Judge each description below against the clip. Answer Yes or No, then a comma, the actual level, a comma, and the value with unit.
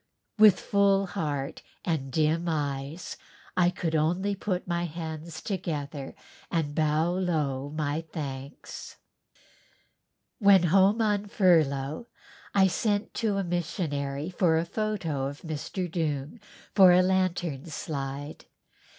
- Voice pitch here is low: No, medium, 165 Hz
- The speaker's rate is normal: No, slow, 115 wpm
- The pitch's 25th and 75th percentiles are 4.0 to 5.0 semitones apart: Yes, average, 4.3 semitones